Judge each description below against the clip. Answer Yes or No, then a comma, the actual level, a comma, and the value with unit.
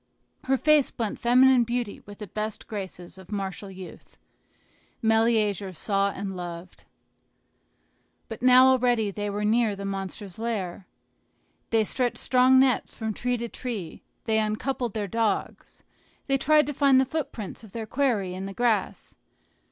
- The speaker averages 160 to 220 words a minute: No, average, 150 wpm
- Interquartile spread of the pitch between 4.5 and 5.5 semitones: No, average, 3.9 semitones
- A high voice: Yes, high, 220 Hz